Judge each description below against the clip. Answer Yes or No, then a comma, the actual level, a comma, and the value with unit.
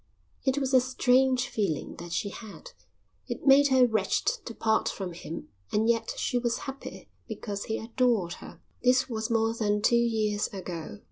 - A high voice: Yes, high, 230 Hz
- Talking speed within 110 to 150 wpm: No, average, 175 wpm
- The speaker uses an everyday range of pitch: Yes, average, 3.6 semitones